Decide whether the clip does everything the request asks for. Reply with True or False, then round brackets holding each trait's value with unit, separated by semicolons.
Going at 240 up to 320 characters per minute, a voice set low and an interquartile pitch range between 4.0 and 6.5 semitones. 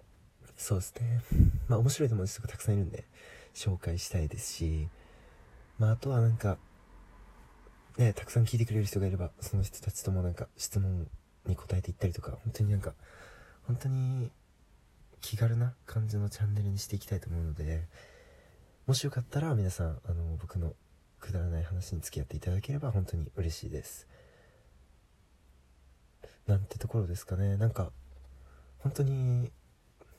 False (330 characters per minute; 95 Hz; 5.3 semitones)